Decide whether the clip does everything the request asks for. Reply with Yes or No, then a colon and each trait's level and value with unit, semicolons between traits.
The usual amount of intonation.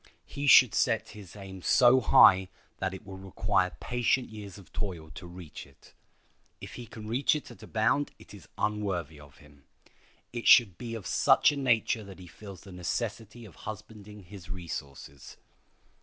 Yes: average, 3.8 semitones